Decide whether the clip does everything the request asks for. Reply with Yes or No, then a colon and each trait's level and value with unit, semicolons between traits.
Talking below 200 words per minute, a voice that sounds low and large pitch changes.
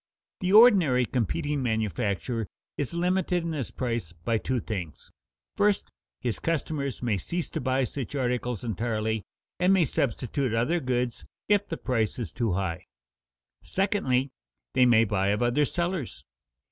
Yes: average, 145 wpm; low, 125 Hz; wide, 6.5 semitones